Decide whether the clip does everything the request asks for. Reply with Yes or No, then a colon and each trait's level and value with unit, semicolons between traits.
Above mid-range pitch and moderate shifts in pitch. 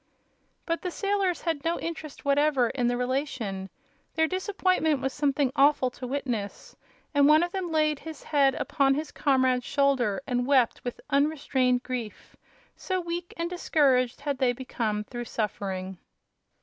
Yes: very high, 280 Hz; average, 4.1 semitones